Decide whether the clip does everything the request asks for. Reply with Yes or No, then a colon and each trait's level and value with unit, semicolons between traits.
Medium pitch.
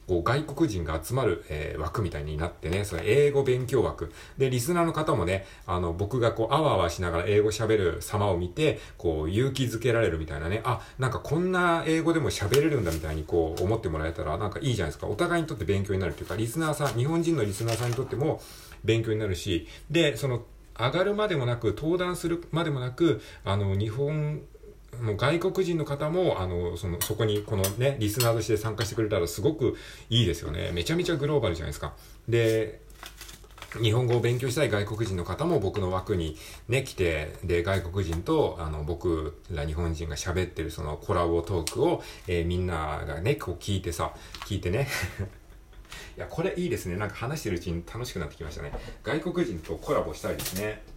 No: low, 110 Hz